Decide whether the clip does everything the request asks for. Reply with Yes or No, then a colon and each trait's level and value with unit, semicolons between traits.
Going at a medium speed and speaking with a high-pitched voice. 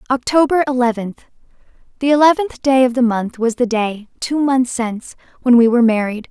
Yes: average, 160 wpm; very high, 250 Hz